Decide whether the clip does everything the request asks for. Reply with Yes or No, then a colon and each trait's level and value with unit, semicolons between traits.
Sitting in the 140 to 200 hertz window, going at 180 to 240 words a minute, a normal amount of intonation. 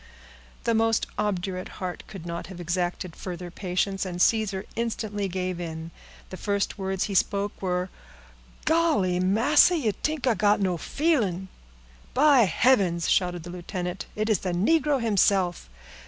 No: high, 190 Hz; average, 145 wpm; average, 3.6 semitones